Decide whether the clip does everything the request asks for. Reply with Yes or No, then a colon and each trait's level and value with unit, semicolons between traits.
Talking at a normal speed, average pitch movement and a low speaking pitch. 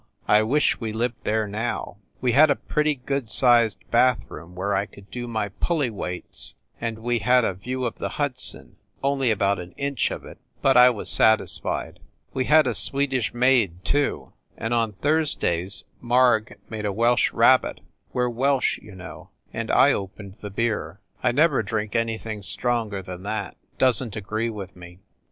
Yes: average, 180 wpm; average, 3.8 semitones; low, 115 Hz